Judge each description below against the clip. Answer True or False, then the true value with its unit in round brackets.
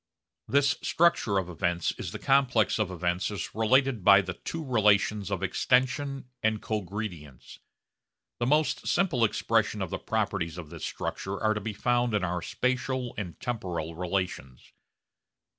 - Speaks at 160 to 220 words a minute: False (150 wpm)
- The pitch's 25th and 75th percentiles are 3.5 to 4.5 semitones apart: False (5.4 semitones)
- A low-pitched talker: True (105 Hz)